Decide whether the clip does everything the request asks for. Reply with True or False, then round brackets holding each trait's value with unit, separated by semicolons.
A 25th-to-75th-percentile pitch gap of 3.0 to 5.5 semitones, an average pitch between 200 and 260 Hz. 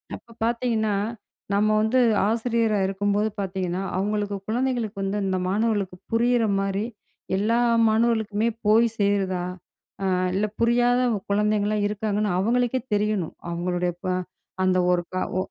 False (2.6 semitones; 210 Hz)